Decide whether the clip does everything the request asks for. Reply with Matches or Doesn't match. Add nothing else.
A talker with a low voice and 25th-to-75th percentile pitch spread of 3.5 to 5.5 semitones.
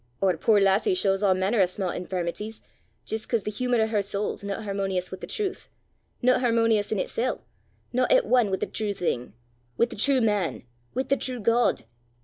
Doesn't match